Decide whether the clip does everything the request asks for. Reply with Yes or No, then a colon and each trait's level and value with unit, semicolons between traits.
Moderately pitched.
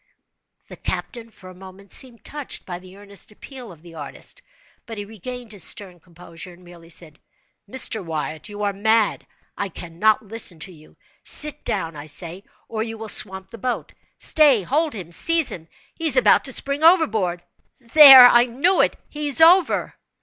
No: high, 210 Hz